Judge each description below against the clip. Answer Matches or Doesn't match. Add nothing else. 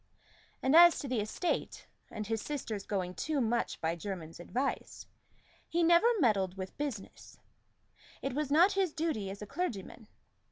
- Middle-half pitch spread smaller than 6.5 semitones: Doesn't match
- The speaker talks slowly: Doesn't match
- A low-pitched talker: Doesn't match